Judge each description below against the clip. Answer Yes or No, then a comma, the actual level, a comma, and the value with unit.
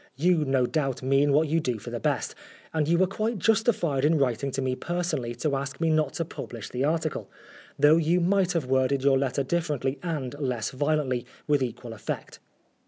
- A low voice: No, medium, 145 Hz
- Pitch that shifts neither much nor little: Yes, average, 4.0 semitones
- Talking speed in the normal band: Yes, average, 195 wpm